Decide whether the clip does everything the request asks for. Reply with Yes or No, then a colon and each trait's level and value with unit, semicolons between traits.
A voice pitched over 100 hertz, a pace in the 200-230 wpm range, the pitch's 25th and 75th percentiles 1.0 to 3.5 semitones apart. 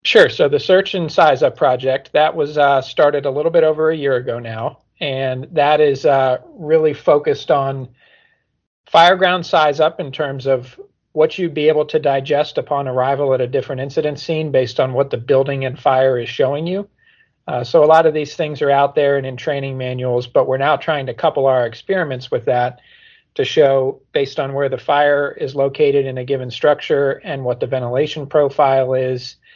Yes: medium, 140 Hz; fast, 205 wpm; average, 3.0 semitones